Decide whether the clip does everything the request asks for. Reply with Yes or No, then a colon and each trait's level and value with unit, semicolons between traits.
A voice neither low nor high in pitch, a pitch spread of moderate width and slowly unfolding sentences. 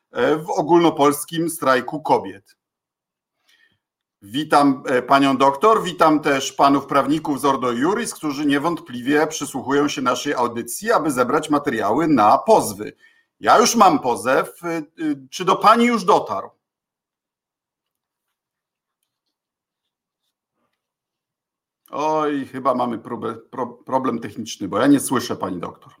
Yes: medium, 150 Hz; average, 3.0 semitones; slow, 105 wpm